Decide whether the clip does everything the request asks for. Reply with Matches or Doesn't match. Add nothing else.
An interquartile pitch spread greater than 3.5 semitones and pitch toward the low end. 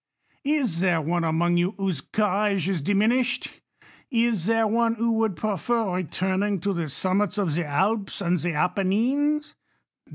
Doesn't match